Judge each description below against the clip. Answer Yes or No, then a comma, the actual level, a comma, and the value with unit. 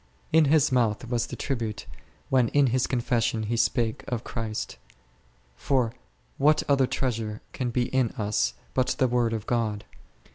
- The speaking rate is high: No, average, 155 wpm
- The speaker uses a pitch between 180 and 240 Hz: No, low, 120 Hz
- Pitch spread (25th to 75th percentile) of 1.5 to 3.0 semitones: Yes, narrow, 2.6 semitones